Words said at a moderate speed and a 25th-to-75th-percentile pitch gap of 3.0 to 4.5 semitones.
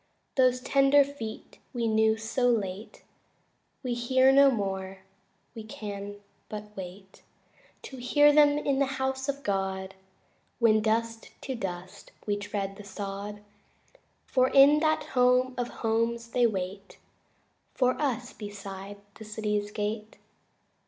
No: slow, 130 wpm; average, 4.1 semitones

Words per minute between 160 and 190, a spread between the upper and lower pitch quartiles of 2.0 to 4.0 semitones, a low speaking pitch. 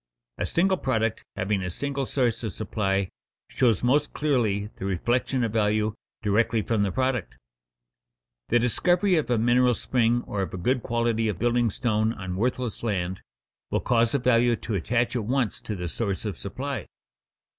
Yes: average, 175 wpm; average, 3.2 semitones; low, 115 Hz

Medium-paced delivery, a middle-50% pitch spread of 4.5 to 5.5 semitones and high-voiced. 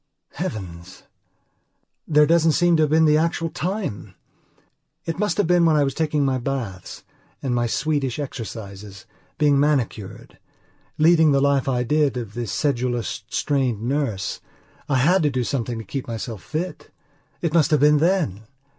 No: average, 160 wpm; average, 5.0 semitones; medium, 140 Hz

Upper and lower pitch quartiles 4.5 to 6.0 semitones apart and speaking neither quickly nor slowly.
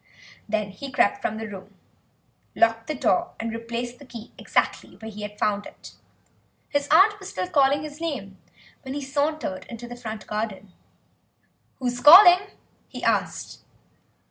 Yes: average, 5.2 semitones; average, 155 wpm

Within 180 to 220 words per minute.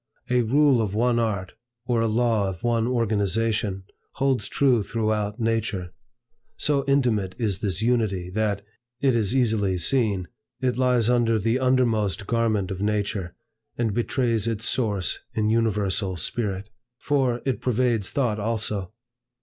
No: average, 140 wpm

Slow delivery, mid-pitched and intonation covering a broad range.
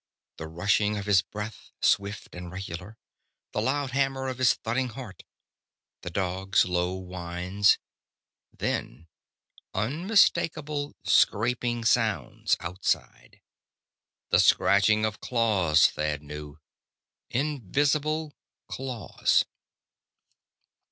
No: slow, 90 wpm; low, 105 Hz; wide, 6.4 semitones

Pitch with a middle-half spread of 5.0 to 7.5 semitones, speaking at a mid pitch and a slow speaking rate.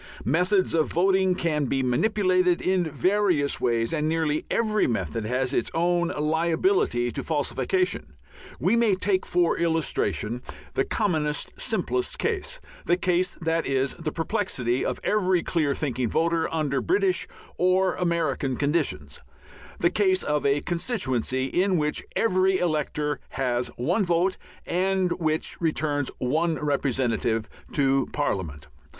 Yes: average, 5.3 semitones; medium, 160 Hz; slow, 130 wpm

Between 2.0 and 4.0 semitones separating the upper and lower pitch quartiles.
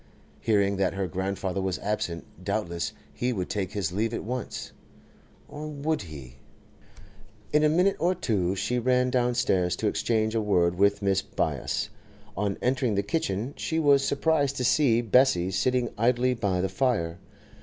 No: average, 5.1 semitones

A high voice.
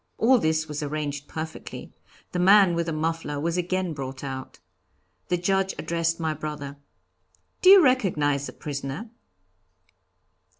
No: medium, 160 Hz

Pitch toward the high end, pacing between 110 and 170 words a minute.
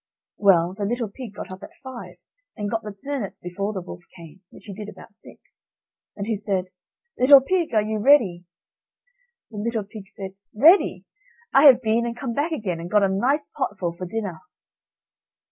No: high, 210 Hz; average, 185 wpm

